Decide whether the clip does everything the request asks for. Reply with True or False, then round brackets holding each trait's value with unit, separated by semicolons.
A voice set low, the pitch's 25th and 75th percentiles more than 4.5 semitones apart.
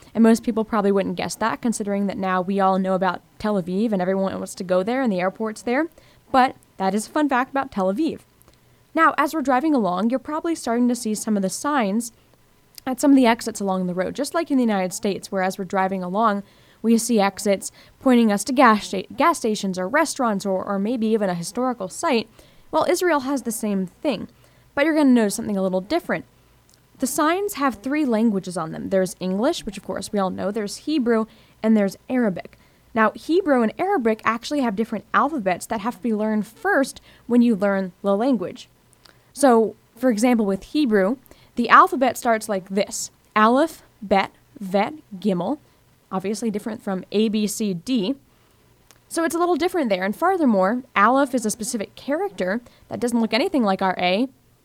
False (220 Hz; 5.0 semitones)